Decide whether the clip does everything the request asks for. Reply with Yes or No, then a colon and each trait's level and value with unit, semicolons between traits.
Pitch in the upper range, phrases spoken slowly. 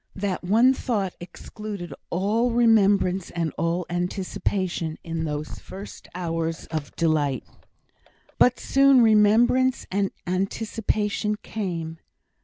Yes: high, 195 Hz; slow, 100 wpm